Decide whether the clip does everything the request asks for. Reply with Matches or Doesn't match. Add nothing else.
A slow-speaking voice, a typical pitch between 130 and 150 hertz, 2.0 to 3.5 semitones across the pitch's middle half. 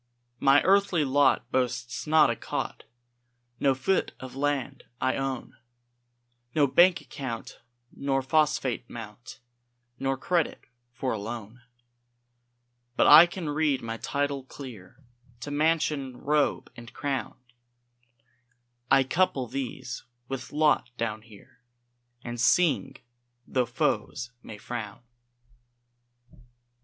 Matches